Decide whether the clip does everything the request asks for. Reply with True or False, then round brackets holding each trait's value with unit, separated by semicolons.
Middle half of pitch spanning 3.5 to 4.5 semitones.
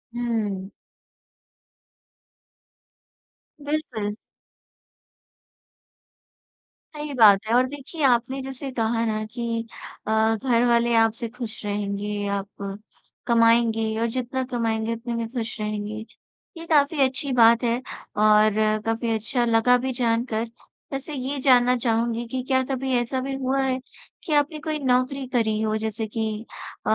False (2.9 semitones)